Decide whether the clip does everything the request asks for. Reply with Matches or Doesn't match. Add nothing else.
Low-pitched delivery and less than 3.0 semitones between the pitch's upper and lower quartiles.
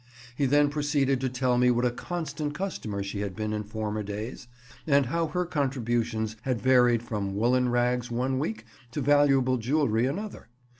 Doesn't match